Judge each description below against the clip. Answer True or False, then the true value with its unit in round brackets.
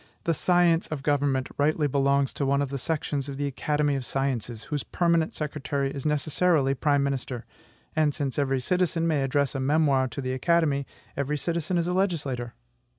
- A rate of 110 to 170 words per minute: False (180 wpm)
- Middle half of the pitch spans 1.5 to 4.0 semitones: True (2.6 semitones)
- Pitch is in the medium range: True (145 Hz)